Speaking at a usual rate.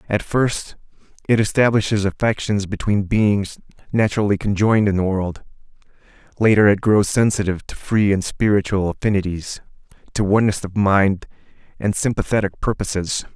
No: slow, 125 wpm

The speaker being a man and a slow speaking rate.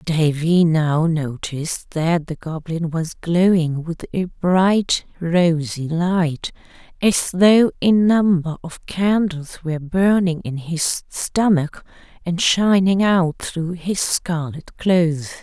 No: female; slow, 120 wpm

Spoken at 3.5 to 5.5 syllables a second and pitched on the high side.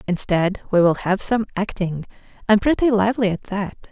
Yes: 5.0 syllables/s; high, 200 Hz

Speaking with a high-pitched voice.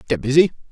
No: low, 135 Hz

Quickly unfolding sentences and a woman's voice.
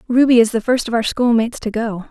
Yes: fast, 255 wpm; female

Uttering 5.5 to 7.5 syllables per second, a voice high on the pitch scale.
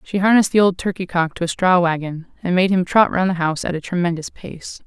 No: 6.0 syllables/s; medium, 180 Hz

